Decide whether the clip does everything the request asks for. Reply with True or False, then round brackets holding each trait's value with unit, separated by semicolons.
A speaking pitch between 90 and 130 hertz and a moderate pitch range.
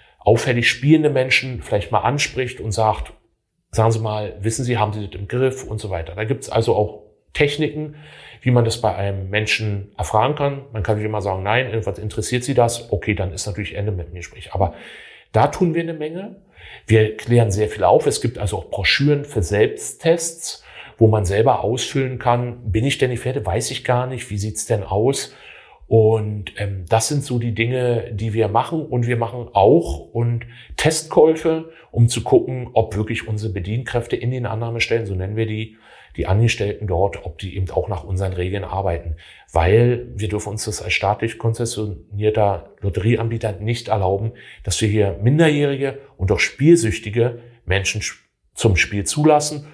True (110 Hz; 3.3 semitones)